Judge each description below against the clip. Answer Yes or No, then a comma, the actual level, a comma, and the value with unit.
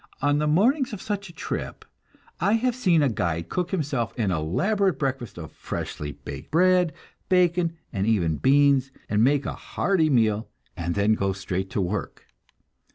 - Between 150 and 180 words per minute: Yes, average, 165 wpm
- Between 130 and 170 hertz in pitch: Yes, medium, 140 Hz